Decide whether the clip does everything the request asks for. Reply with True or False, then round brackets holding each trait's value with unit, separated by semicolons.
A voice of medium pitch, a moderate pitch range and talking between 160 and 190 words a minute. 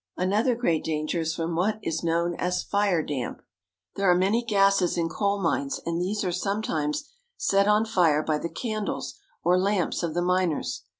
True (180 Hz; 3.5 semitones; 180 wpm)